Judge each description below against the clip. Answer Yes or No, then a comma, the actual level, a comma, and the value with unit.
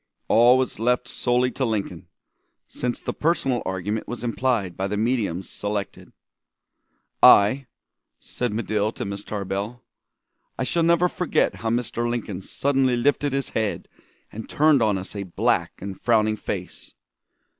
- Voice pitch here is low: Yes, low, 115 Hz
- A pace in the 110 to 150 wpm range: Yes, average, 145 wpm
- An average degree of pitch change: Yes, average, 3.8 semitones